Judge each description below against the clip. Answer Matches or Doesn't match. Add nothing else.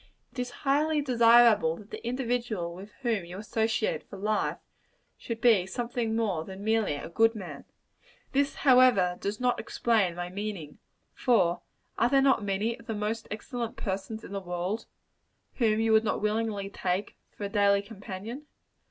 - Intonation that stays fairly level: Doesn't match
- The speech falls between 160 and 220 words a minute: Matches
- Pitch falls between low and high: Doesn't match